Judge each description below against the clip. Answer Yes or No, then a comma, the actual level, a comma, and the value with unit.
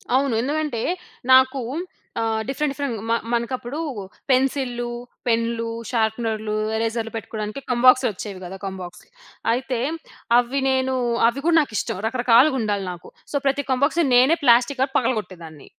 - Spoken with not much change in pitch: No, average, 3.1 semitones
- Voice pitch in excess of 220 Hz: Yes, high, 240 Hz